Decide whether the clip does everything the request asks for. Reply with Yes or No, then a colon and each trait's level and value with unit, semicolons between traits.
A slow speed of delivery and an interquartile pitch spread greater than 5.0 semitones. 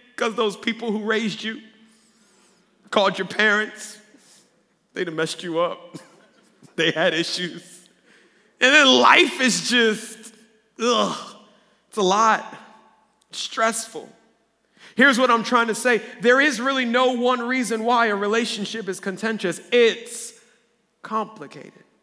No: slow, 130 wpm; narrow, 2.6 semitones